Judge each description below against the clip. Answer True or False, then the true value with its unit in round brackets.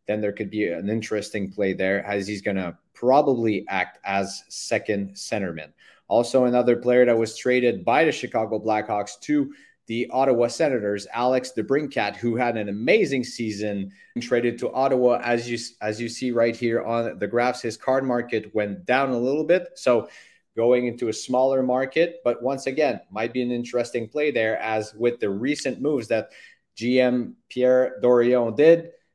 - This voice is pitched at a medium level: False (120 Hz)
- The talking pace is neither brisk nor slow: True (175 wpm)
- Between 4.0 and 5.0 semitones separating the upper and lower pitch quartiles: False (3.1 semitones)